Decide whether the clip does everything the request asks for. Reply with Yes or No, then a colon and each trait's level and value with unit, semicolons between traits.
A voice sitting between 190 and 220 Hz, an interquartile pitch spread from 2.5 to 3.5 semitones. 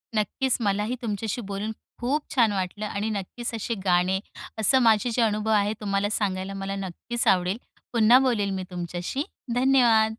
Yes: high, 210 Hz; average, 3.1 semitones